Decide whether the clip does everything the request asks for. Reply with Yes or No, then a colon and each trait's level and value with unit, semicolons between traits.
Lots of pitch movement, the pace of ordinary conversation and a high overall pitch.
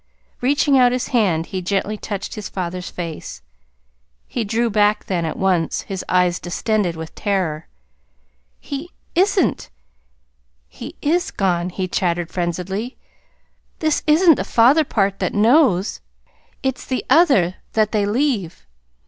No: wide, 6.0 semitones; slow, 130 wpm; high, 205 Hz